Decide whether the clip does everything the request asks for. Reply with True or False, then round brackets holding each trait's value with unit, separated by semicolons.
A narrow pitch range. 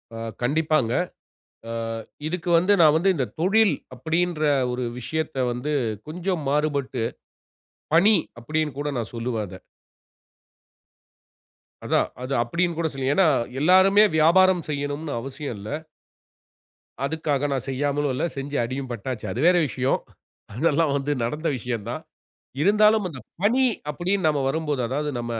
False (4.5 semitones)